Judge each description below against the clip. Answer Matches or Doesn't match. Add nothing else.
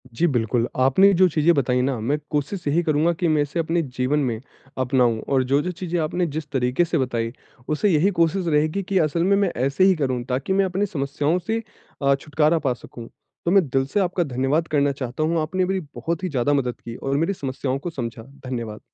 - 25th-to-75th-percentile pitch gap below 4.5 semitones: Doesn't match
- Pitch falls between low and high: Matches